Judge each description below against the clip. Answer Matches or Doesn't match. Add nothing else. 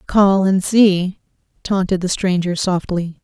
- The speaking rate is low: Matches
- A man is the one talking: Doesn't match